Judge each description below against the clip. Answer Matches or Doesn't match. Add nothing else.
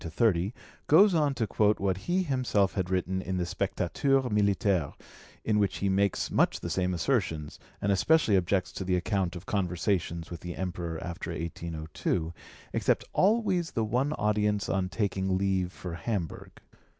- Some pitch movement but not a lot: Matches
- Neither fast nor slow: Matches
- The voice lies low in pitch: Matches